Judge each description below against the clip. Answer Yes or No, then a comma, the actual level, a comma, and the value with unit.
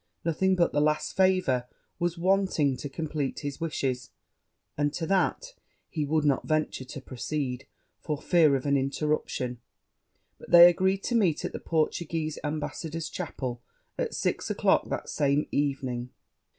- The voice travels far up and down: No, average, 3.7 semitones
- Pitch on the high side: No, medium, 150 Hz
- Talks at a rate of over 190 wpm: No, average, 150 wpm